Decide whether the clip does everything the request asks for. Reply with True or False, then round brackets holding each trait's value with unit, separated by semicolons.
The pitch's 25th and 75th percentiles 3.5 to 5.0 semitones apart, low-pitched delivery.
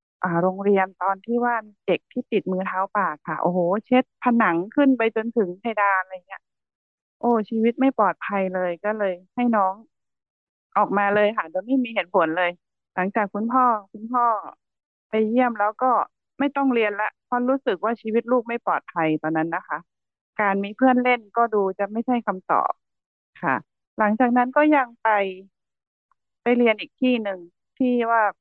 False (4.2 semitones; 215 Hz)